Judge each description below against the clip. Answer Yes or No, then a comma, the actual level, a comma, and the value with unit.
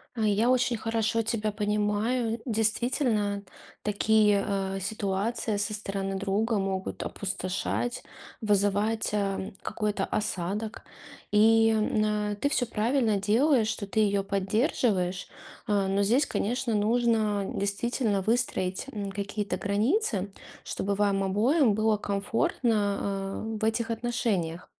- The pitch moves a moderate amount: No, narrow, 2.1 semitones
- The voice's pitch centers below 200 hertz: No, high, 210 Hz